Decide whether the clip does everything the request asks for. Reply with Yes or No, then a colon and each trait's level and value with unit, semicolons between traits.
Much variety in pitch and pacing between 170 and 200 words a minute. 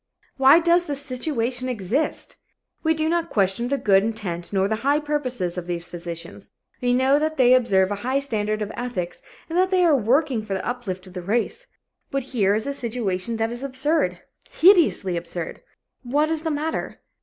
Yes: wide, 6.6 semitones; average, 190 wpm